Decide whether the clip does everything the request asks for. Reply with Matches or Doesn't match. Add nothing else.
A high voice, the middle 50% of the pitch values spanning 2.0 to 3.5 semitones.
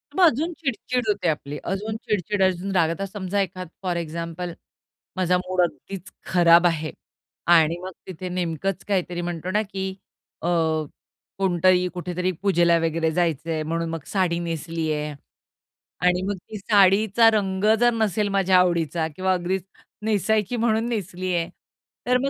Doesn't match